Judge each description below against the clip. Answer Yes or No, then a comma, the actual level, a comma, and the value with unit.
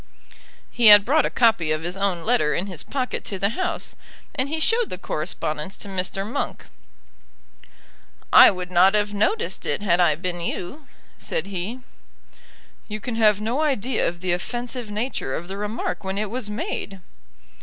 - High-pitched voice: Yes, high, 205 Hz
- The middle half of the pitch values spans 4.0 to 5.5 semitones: Yes, average, 5.0 semitones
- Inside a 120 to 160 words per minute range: No, average, 175 wpm